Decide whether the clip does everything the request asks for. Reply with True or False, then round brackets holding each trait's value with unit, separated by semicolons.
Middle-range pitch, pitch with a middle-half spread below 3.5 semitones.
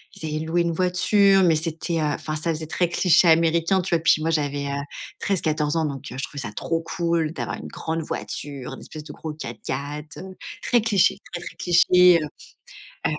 True (160 Hz; 2.6 semitones)